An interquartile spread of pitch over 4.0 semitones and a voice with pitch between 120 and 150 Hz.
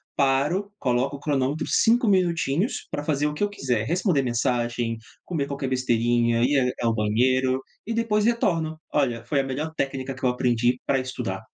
Yes: average, 4.4 semitones; low, 135 Hz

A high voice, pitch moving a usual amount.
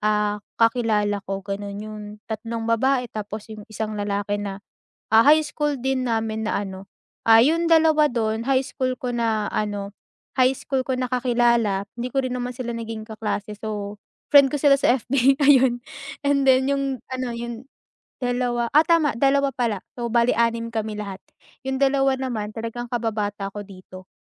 Yes: high, 235 Hz; average, 3.6 semitones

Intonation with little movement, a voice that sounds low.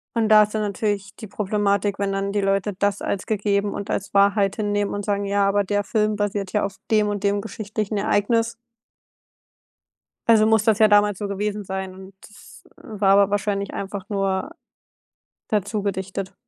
No: narrow, 1.1 semitones; high, 205 Hz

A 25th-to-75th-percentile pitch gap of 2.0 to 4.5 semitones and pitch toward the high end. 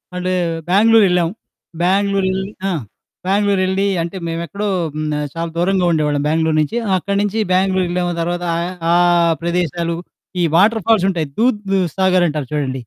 No: average, 2.8 semitones; medium, 180 Hz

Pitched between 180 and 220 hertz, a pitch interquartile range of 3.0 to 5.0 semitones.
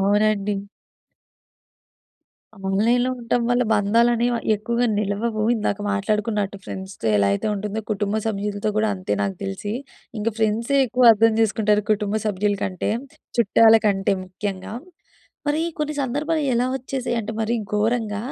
No: high, 215 Hz; narrow, 2.6 semitones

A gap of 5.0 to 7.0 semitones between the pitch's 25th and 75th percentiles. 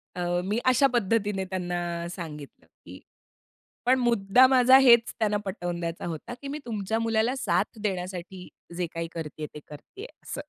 Yes: wide, 5.4 semitones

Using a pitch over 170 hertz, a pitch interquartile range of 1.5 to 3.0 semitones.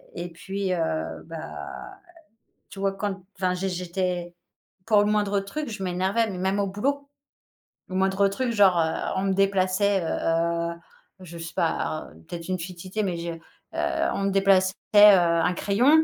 Yes: high, 190 Hz; narrow, 2.4 semitones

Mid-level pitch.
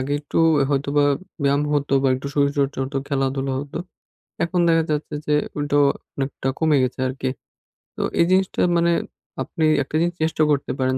Yes: medium, 145 Hz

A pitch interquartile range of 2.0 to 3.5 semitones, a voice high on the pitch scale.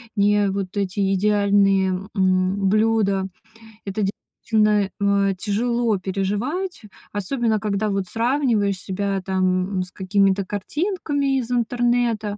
Yes: narrow, 2.6 semitones; high, 205 Hz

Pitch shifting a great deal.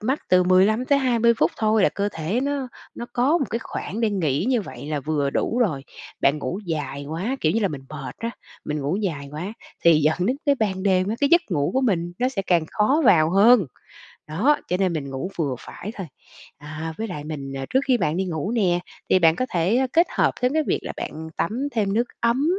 Yes: wide, 7.1 semitones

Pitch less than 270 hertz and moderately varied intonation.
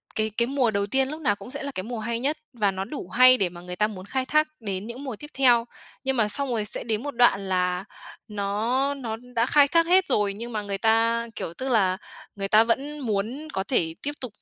Yes: high, 230 Hz; average, 4.8 semitones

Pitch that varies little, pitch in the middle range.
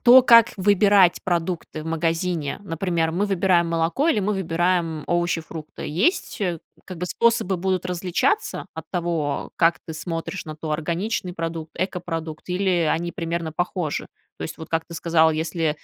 Yes: narrow, 2.3 semitones; medium, 170 Hz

